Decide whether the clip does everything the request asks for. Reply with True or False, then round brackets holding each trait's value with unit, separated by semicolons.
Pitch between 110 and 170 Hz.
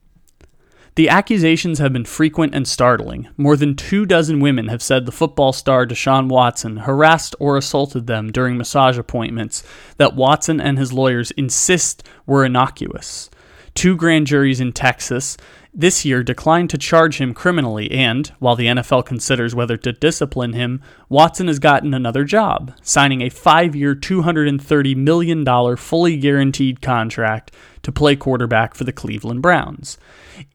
True (135 Hz)